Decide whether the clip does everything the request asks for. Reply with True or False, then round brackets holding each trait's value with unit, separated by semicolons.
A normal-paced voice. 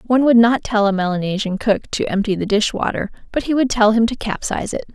False (245 wpm)